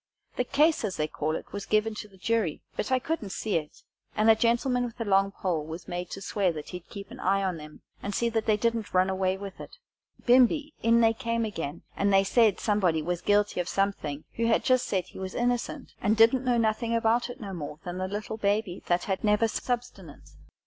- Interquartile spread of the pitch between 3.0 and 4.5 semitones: Yes, average, 3.7 semitones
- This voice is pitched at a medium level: No, high, 205 Hz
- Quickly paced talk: Yes, fast, 230 wpm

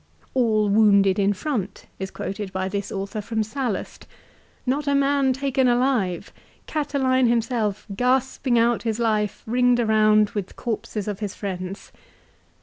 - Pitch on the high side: Yes, high, 220 Hz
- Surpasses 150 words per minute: No, average, 145 wpm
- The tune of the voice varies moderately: Yes, average, 3.9 semitones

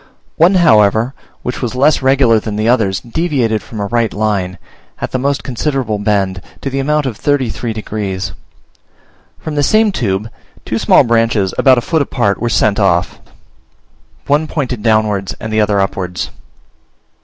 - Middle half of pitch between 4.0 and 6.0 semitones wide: Yes, average, 4.7 semitones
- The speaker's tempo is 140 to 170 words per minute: Yes, average, 165 wpm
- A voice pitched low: Yes, low, 115 Hz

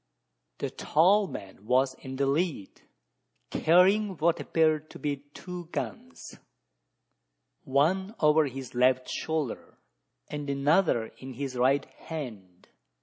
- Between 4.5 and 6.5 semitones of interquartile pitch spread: No, average, 4.1 semitones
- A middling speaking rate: No, slow, 115 wpm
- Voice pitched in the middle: Yes, medium, 145 Hz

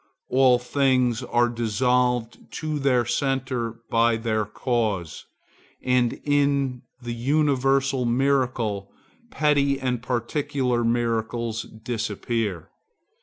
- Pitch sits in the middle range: No, low, 125 Hz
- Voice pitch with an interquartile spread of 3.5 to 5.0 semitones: No, narrow, 2.5 semitones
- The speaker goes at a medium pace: No, slow, 90 wpm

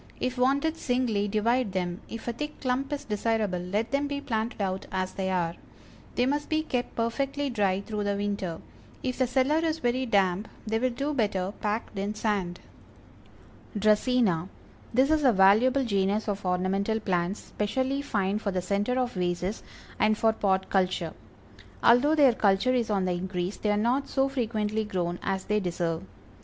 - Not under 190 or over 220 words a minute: No, average, 175 wpm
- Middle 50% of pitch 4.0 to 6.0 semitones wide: Yes, average, 4.8 semitones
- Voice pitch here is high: Yes, high, 215 Hz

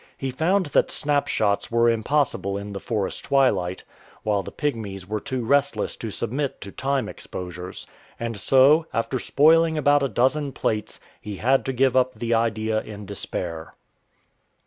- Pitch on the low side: Yes, low, 120 Hz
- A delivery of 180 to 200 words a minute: No, average, 155 wpm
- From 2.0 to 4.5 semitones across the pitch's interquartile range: No, average, 5.3 semitones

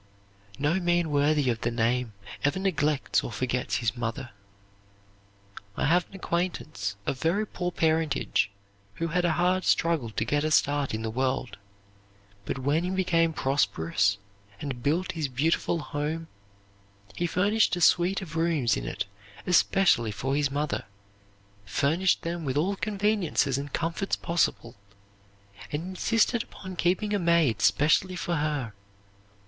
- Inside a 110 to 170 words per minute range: Yes, average, 145 wpm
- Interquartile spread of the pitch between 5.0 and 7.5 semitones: Yes, wide, 5.4 semitones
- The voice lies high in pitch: No, medium, 155 Hz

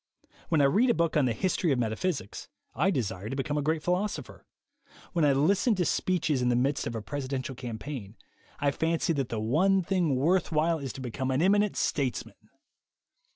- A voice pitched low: No, medium, 145 Hz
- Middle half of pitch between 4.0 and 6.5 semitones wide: Yes, average, 5.1 semitones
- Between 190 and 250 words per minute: Yes, average, 195 wpm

